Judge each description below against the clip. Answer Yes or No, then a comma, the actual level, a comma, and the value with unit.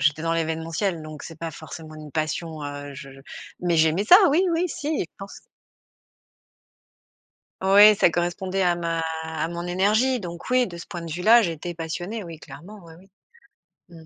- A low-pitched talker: No, medium, 170 Hz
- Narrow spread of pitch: No, average, 3.3 semitones